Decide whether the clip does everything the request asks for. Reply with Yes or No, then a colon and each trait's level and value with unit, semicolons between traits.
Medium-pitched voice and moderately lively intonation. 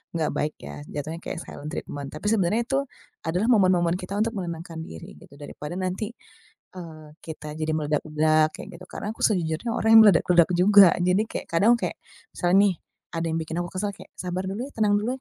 Yes: medium, 175 Hz; average, 4.1 semitones